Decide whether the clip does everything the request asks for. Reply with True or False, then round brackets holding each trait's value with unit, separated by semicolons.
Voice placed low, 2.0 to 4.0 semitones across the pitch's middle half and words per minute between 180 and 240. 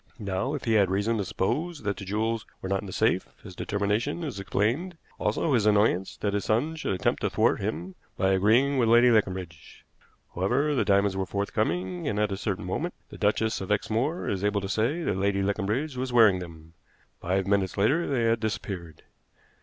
True (105 Hz; 3.5 semitones; 200 wpm)